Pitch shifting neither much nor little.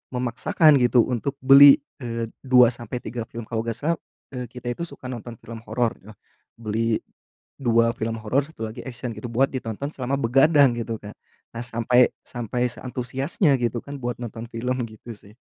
No: narrow, 2.2 semitones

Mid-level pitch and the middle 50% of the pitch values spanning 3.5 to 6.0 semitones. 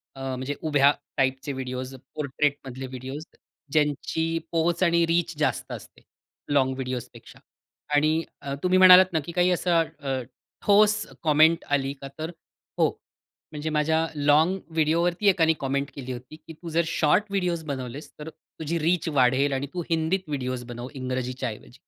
Yes: medium, 150 Hz; average, 3.8 semitones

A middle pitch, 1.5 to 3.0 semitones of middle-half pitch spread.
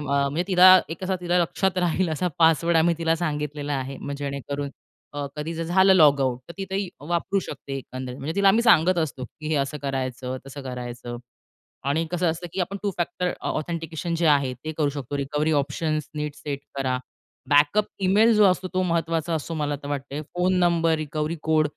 No: medium, 155 Hz; average, 3.7 semitones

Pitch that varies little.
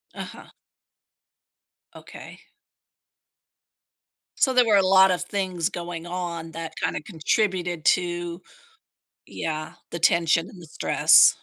Yes: narrow, 2.3 semitones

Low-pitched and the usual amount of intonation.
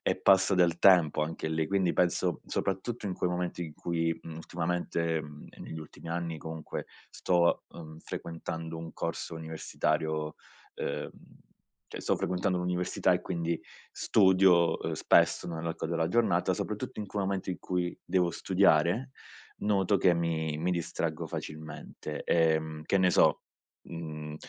No: very low, 85 Hz; narrow, 2.2 semitones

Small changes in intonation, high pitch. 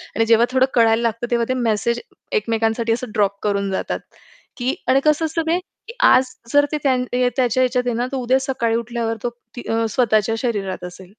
Yes: narrow, 2.3 semitones; high, 235 Hz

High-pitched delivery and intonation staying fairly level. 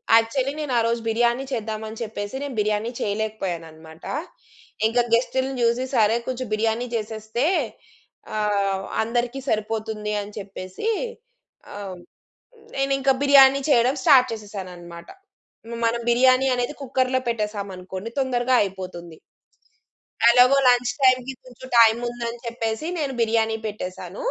No: high, 230 Hz; average, 3.4 semitones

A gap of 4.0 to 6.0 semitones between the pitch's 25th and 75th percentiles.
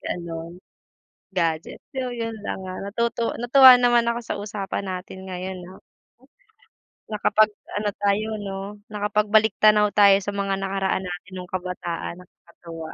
No: average, 2.9 semitones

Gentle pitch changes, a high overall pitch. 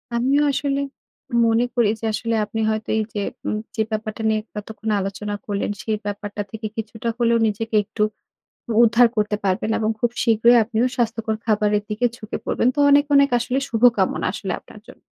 Yes: narrow, 1.9 semitones; high, 220 Hz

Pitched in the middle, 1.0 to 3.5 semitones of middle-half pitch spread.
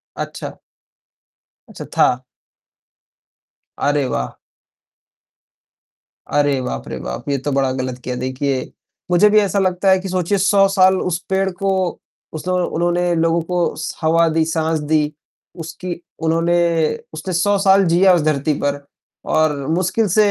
No: medium, 165 Hz; average, 4.3 semitones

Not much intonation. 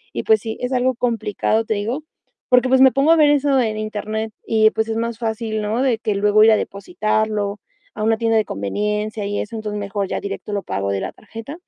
Yes: narrow, 2.0 semitones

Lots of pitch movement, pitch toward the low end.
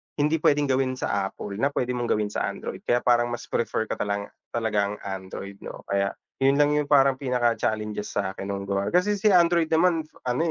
Yes: wide, 6.1 semitones; low, 120 Hz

